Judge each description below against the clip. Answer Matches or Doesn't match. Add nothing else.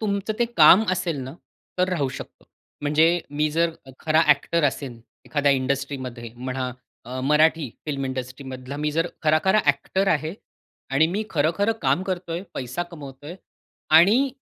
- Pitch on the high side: Doesn't match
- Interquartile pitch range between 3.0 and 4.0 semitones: Doesn't match